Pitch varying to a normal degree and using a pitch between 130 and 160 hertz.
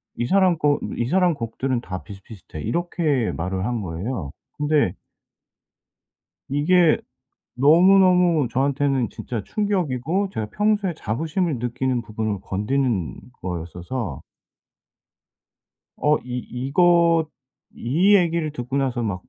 No: wide, 7.1 semitones; low, 135 Hz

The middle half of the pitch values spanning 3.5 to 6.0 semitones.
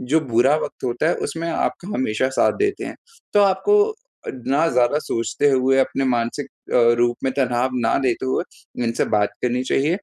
Yes: average, 4.0 semitones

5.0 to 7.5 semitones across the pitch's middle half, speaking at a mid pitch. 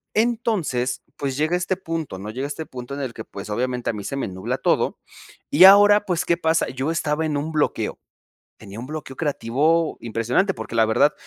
Yes: average, 5.3 semitones; medium, 145 Hz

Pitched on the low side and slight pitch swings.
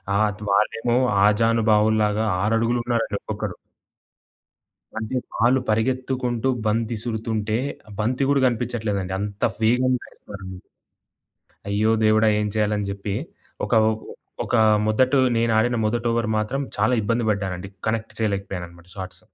Yes: low, 110 Hz; narrow, 2.3 semitones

